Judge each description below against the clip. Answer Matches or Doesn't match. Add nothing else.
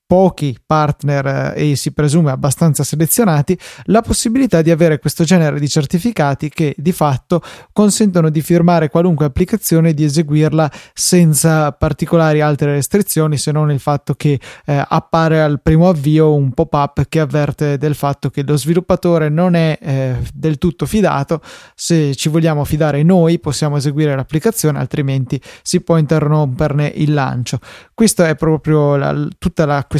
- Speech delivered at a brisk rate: Doesn't match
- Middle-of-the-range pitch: Matches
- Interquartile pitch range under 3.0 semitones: Matches